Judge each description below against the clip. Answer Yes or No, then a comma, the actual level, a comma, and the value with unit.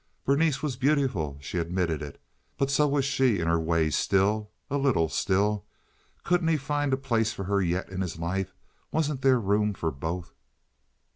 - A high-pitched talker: No, low, 105 Hz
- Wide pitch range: Yes, wide, 8.0 semitones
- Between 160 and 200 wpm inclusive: Yes, average, 170 wpm